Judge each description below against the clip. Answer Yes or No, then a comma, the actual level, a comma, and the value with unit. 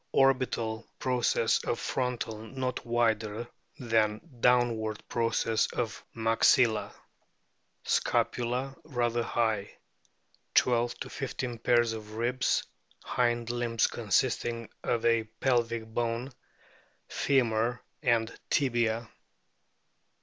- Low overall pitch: Yes, low, 120 Hz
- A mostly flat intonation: Yes, narrow, 1.5 semitones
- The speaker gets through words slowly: Yes, slow, 90 wpm